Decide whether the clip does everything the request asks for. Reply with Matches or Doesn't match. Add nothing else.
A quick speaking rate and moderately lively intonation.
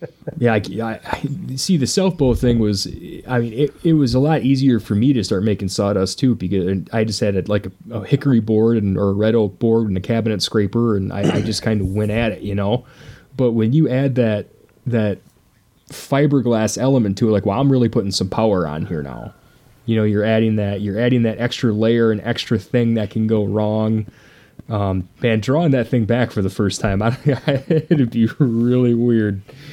Matches